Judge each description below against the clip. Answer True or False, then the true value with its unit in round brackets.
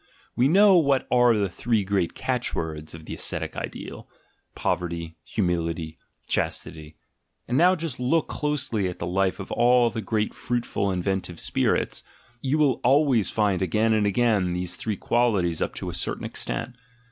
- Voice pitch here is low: True (110 Hz)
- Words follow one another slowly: False (170 wpm)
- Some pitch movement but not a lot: False (5.7 semitones)